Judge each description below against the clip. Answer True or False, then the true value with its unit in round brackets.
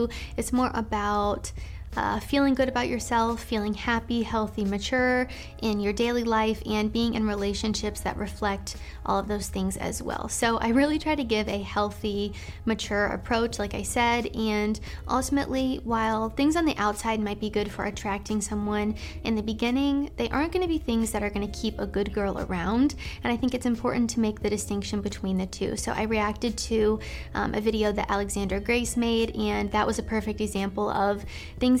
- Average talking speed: True (195 wpm)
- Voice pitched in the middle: False (220 Hz)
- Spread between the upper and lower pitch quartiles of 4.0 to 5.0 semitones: False (2.4 semitones)